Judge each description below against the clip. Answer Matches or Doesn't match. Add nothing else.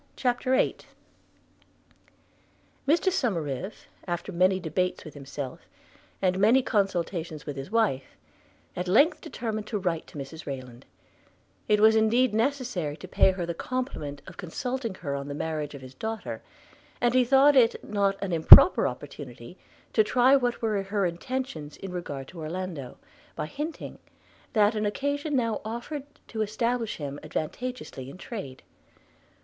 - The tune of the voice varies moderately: Doesn't match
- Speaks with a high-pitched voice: Matches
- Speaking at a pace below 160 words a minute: Matches